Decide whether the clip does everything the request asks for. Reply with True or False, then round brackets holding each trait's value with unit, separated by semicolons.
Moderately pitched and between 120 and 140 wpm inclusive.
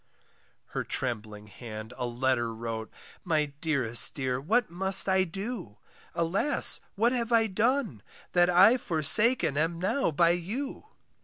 True (170 Hz; 135 wpm)